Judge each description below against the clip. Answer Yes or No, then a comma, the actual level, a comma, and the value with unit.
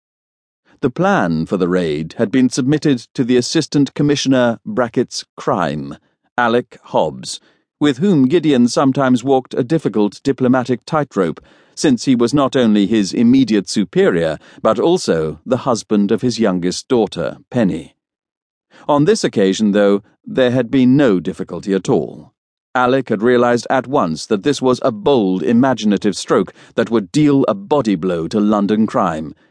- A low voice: Yes, low, 125 Hz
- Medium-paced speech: Yes, average, 150 wpm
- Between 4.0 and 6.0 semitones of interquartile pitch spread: Yes, average, 4.8 semitones